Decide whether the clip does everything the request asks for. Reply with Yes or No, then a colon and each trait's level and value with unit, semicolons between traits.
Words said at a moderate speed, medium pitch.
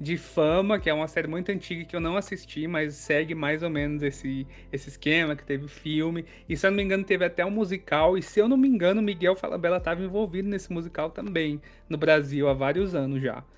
No: fast, 235 wpm; medium, 165 Hz